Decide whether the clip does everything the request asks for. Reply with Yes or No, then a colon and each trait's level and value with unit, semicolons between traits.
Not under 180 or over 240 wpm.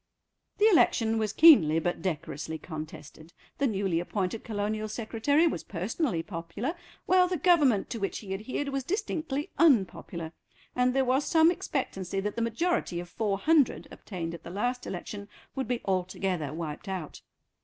No: average, 155 wpm